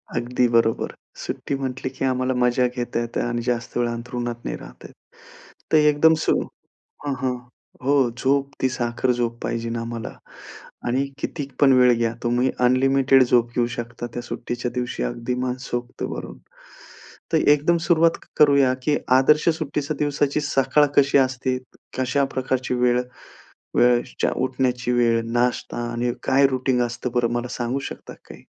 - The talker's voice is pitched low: Yes, low, 125 Hz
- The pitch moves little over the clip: Yes, narrow, 2.0 semitones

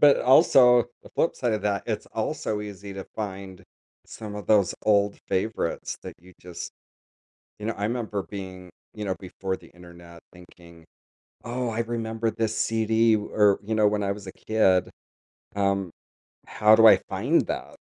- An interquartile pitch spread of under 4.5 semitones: Yes, average, 2.8 semitones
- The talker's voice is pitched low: Yes, low, 105 Hz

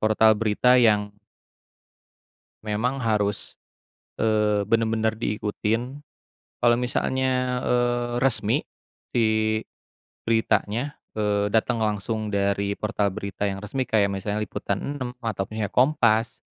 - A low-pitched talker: Yes, low, 110 Hz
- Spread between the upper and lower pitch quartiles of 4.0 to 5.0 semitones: No, average, 2.7 semitones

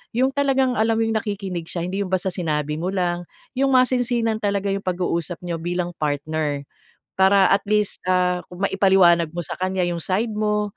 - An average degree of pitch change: Yes, average, 3.6 semitones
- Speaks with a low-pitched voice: No, high, 190 Hz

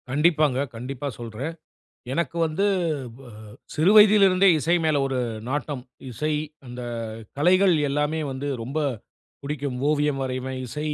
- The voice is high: No, medium, 145 Hz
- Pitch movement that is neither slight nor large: Yes, average, 3.4 semitones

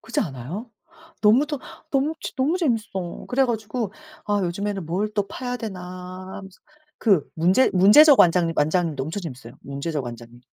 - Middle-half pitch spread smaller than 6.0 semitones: Yes, wide, 5.6 semitones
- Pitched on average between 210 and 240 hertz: No, high, 190 Hz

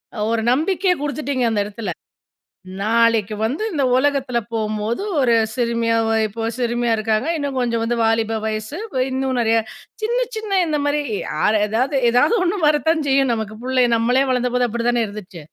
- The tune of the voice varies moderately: Yes, average, 3.9 semitones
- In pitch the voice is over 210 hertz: Yes, high, 240 Hz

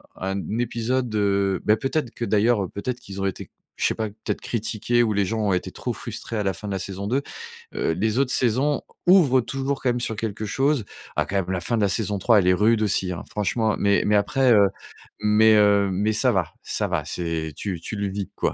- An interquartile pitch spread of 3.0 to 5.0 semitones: Yes, average, 3.3 semitones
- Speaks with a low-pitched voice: Yes, low, 105 Hz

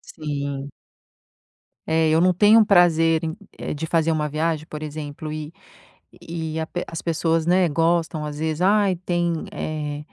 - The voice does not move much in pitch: Yes, narrow, 2.0 semitones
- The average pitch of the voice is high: No, medium, 160 Hz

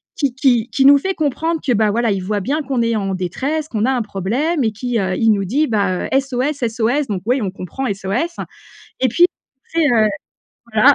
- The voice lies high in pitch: Yes, high, 240 Hz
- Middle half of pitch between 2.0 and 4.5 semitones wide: No, average, 5.1 semitones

